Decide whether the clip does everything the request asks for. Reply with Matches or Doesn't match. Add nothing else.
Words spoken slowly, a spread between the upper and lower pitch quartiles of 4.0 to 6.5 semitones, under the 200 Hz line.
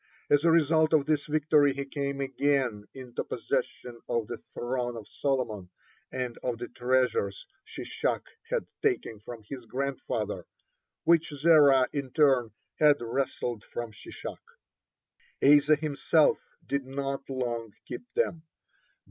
Doesn't match